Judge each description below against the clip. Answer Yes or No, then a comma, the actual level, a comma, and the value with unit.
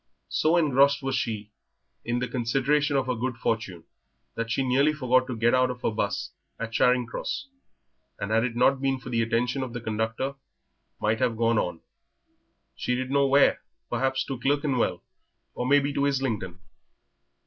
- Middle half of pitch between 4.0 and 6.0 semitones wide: No, average, 3.0 semitones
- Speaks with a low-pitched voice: Yes, low, 125 Hz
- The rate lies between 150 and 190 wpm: Yes, average, 180 wpm